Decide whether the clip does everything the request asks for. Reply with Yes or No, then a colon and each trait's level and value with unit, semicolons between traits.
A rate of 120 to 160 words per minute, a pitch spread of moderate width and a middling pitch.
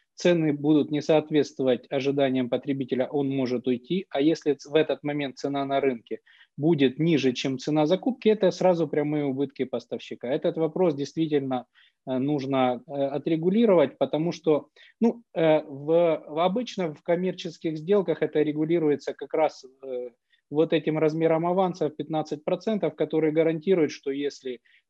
Yes: average, 130 wpm; average, 3.3 semitones; medium, 155 Hz